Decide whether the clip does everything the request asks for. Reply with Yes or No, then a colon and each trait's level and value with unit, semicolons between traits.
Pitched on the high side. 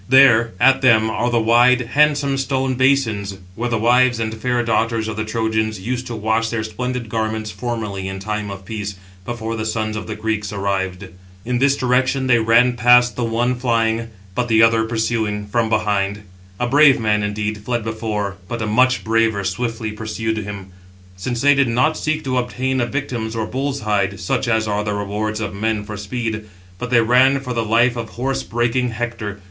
No: low, 115 Hz